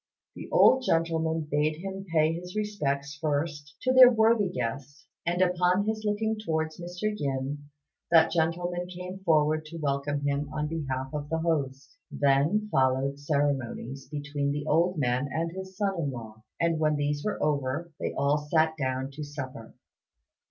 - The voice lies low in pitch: No, medium, 155 Hz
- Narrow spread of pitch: No, average, 3.8 semitones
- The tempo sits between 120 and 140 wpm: No, average, 160 wpm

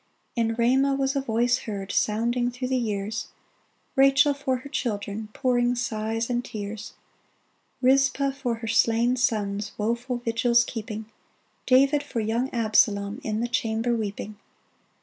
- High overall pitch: Yes, high, 235 Hz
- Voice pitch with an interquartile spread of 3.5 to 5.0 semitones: No, average, 2.8 semitones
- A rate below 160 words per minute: Yes, average, 145 wpm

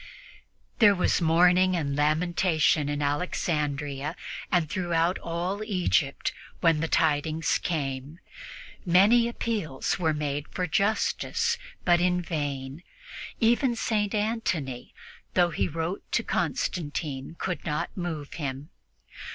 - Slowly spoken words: Yes, slow, 110 wpm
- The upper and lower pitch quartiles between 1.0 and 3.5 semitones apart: No, average, 3.9 semitones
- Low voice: No, medium, 165 Hz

